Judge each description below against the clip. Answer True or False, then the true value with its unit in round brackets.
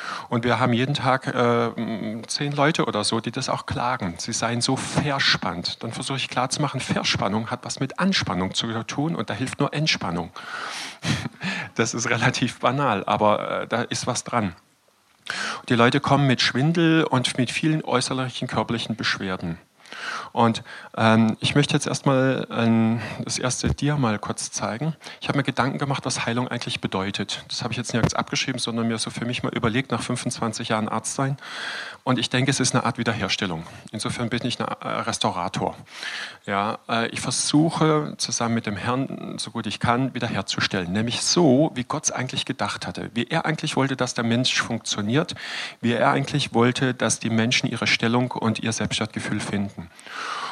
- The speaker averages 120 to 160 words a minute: False (175 wpm)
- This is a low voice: True (120 Hz)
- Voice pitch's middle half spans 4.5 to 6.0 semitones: False (2.9 semitones)